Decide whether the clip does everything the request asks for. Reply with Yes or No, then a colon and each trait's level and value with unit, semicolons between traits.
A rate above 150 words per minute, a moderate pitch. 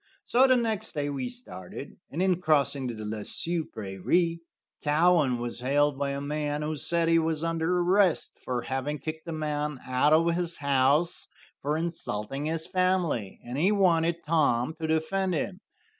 Yes: average, 170 wpm; medium, 155 Hz